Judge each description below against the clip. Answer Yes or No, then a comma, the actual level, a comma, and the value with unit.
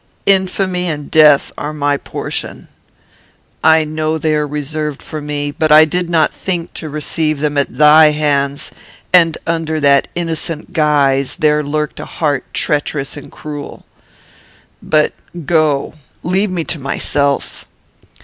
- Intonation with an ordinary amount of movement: No, narrow, 1.8 semitones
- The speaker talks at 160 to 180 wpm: No, average, 140 wpm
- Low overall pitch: No, medium, 150 Hz